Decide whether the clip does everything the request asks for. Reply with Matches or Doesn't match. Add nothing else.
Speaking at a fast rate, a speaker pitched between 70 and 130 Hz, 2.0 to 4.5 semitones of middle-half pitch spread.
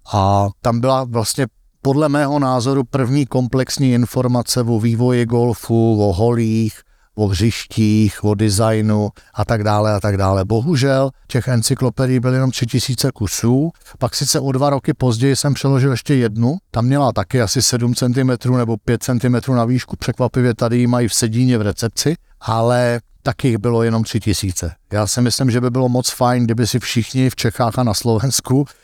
Matches